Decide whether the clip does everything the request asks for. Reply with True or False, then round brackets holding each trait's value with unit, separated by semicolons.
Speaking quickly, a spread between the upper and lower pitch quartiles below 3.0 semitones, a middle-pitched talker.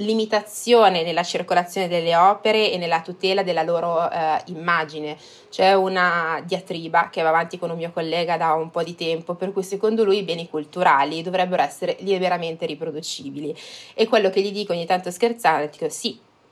True (175 wpm; 2.6 semitones; 175 Hz)